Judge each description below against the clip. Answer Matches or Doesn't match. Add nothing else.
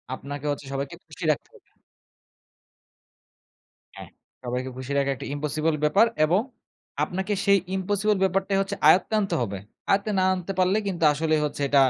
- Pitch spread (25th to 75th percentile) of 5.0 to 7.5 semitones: Matches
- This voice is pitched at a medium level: Matches